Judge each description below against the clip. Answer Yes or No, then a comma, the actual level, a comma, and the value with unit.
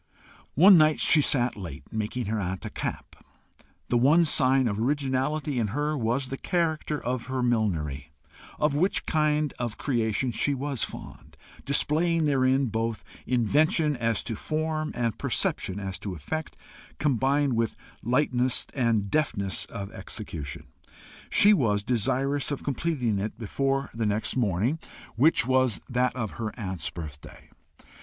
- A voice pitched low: Yes, low, 125 Hz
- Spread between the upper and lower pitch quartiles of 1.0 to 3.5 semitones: No, average, 5.0 semitones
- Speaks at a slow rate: No, average, 145 wpm